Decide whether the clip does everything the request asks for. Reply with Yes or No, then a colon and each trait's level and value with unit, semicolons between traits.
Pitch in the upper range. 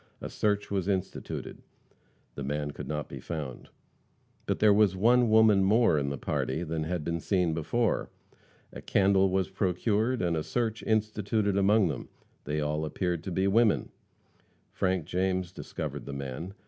No: very low, 95 Hz